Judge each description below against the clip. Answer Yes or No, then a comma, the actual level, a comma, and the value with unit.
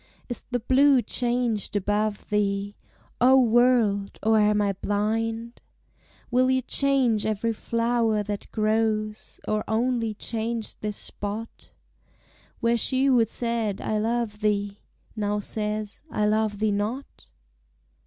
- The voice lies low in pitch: No, high, 220 Hz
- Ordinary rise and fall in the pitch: No, narrow, 2.2 semitones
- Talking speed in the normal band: No, slow, 125 wpm